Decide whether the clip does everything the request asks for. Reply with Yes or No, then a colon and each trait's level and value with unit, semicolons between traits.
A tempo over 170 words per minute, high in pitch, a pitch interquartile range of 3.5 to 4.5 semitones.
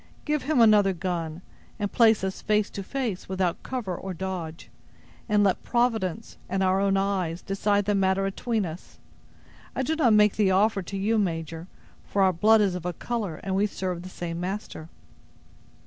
No: average, 180 wpm; high, 195 Hz; average, 2.8 semitones